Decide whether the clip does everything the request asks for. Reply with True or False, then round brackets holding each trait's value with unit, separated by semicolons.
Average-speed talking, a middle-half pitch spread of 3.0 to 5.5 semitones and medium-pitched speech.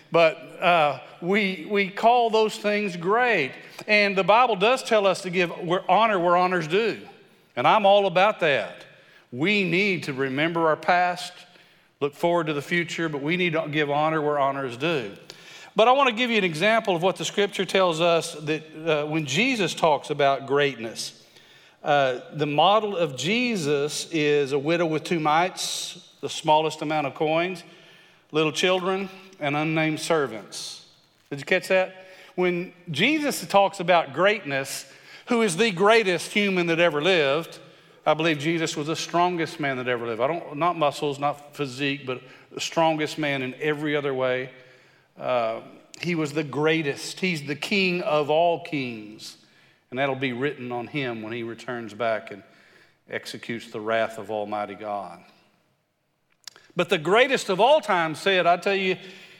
True (170 wpm; 4.3 semitones; 165 Hz)